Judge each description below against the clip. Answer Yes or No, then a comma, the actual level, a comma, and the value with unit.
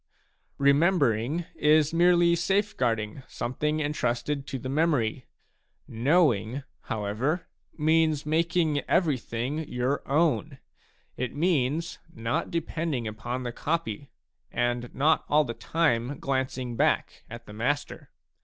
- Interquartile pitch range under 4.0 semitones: No, average, 4.8 semitones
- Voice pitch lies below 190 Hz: Yes, medium, 140 Hz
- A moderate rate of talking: No, slow, 110 wpm